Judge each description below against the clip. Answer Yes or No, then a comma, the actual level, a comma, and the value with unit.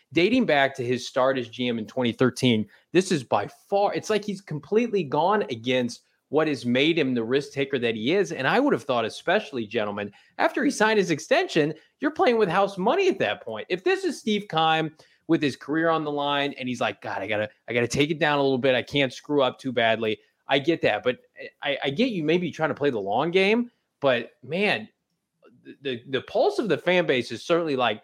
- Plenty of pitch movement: Yes, wide, 7.5 semitones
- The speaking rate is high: Yes, fast, 230 wpm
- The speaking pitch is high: No, medium, 150 Hz